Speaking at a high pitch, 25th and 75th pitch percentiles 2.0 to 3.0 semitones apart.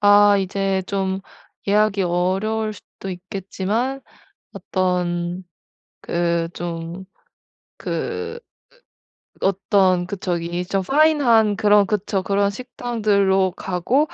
Yes: high, 195 Hz; average, 2.7 semitones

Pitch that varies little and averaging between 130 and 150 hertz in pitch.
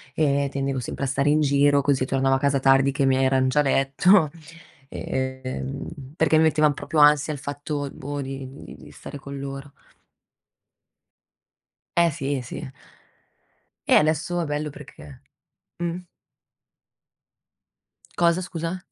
Yes: narrow, 2.2 semitones; medium, 140 Hz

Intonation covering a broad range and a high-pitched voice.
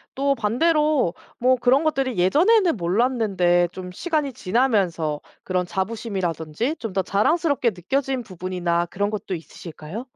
Yes: wide, 6.8 semitones; high, 215 Hz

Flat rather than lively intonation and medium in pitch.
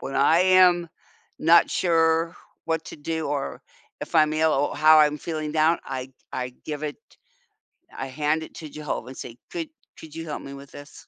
Yes: narrow, 2.2 semitones; medium, 155 Hz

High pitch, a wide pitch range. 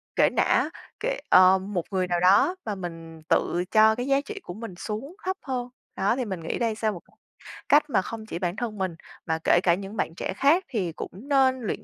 Yes: high, 210 Hz; wide, 6.0 semitones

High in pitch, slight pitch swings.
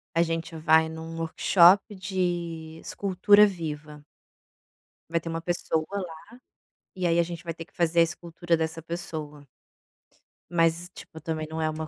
No: medium, 165 Hz; narrow, 1.4 semitones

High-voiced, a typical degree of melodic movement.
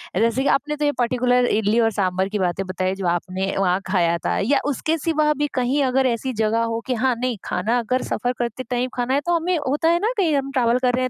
Yes: high, 245 Hz; average, 4.7 semitones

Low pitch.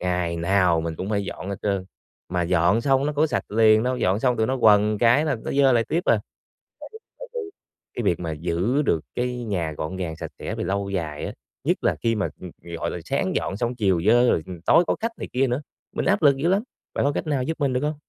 Yes: low, 110 Hz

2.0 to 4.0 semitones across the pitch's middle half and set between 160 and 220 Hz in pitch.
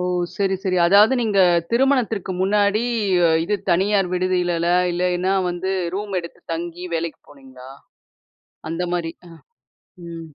Yes: average, 2.9 semitones; medium, 185 Hz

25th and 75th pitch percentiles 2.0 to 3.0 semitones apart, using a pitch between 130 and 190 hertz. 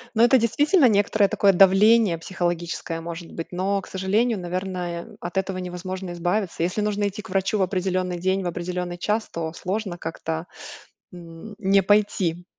Yes: average, 2.7 semitones; medium, 185 Hz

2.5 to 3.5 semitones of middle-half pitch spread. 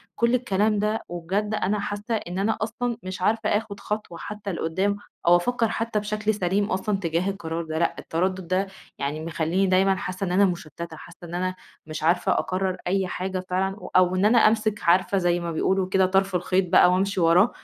Yes: average, 2.9 semitones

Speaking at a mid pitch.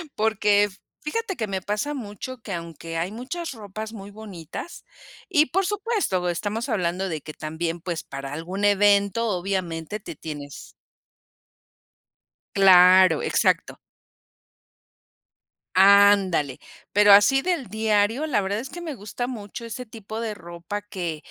No: high, 205 Hz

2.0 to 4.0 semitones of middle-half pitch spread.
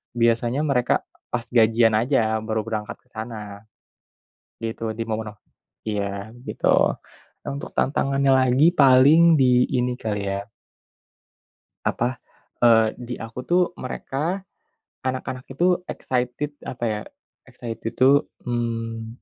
Yes: average, 2.9 semitones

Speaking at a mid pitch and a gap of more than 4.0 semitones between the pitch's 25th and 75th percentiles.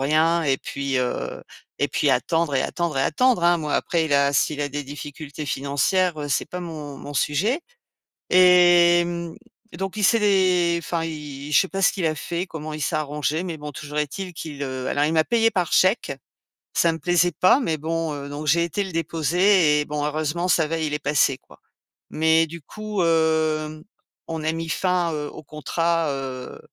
No: medium, 160 Hz; average, 2.9 semitones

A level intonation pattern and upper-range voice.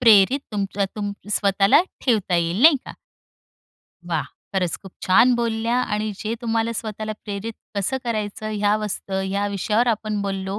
Yes: narrow, 2.3 semitones; high, 210 Hz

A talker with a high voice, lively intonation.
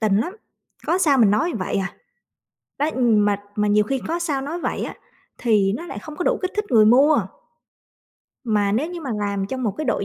Yes: high, 240 Hz; wide, 6.9 semitones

